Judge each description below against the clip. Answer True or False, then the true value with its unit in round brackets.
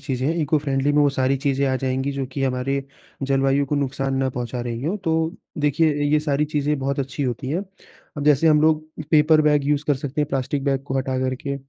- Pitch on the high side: False (140 Hz)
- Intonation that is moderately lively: False (1.9 semitones)